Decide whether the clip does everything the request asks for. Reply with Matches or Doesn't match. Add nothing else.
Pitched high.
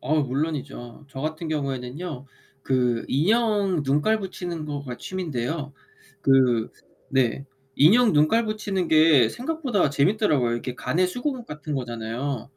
Doesn't match